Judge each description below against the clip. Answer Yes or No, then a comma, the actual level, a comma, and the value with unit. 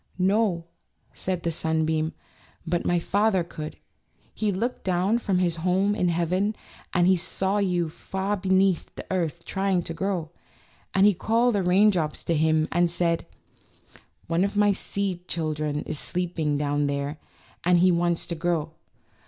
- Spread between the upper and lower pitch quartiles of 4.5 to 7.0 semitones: No, average, 2.9 semitones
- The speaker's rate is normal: Yes, average, 160 wpm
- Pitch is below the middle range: No, medium, 175 Hz